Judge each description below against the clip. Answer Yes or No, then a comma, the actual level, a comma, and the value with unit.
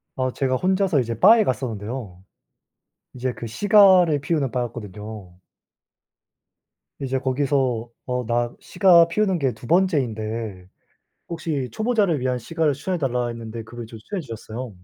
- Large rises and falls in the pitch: Yes, wide, 6.2 semitones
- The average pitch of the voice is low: Yes, low, 130 Hz